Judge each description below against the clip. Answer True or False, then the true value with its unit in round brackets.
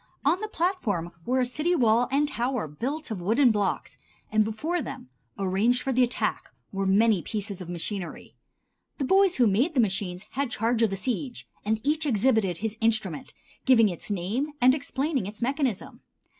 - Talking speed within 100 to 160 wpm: False (175 wpm)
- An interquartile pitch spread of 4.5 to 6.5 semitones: True (5.2 semitones)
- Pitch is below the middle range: False (230 Hz)